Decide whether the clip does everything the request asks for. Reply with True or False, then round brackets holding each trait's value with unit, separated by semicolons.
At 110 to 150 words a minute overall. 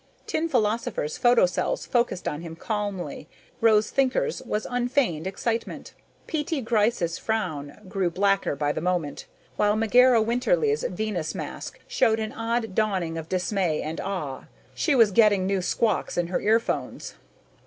True (140 wpm)